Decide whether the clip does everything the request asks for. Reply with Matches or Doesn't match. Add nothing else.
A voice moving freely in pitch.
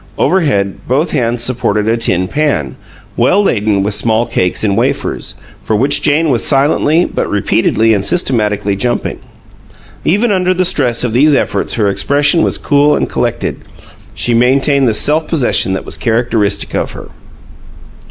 Matches